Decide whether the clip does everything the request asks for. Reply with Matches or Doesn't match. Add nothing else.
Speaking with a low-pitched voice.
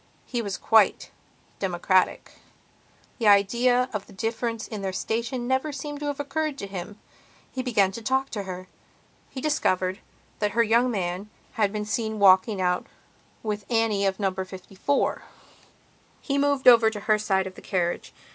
Doesn't match